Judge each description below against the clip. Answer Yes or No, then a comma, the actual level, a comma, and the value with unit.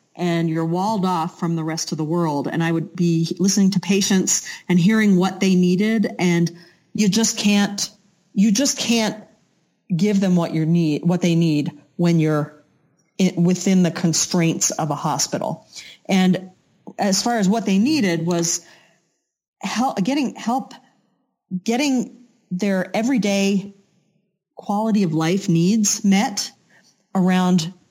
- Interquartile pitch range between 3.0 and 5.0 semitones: Yes, average, 3.3 semitones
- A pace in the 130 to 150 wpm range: Yes, average, 140 wpm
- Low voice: No, medium, 185 Hz